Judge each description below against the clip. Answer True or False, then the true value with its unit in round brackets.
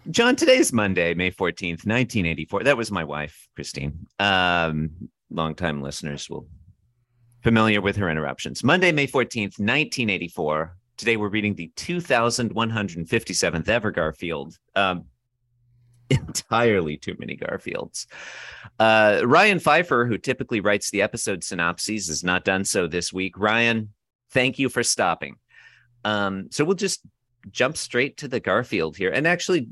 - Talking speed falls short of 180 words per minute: True (135 wpm)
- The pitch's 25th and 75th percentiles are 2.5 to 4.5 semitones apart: False (5.5 semitones)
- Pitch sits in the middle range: False (105 Hz)